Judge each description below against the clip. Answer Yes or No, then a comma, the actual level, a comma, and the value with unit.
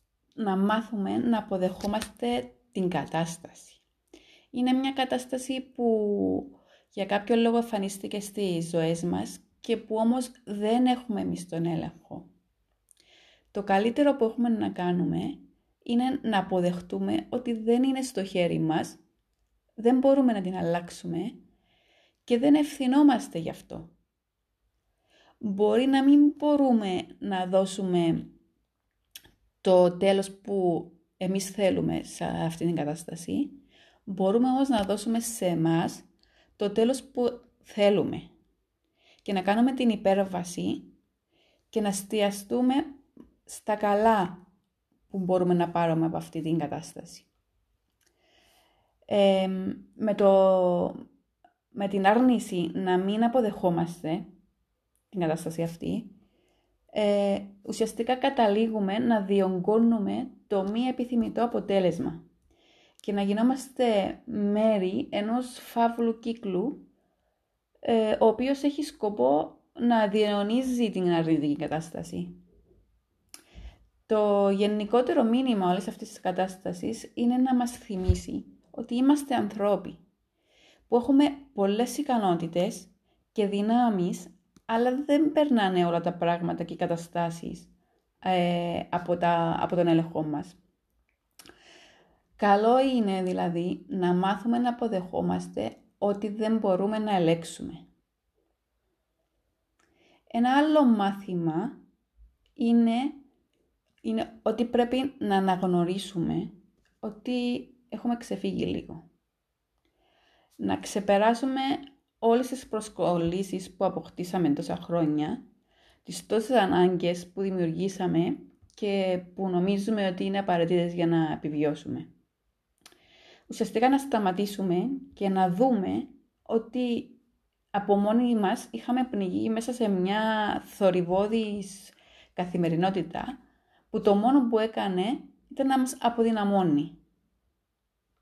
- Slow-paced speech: Yes, slow, 105 wpm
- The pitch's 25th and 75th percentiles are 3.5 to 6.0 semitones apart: Yes, average, 5.1 semitones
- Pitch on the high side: Yes, high, 205 Hz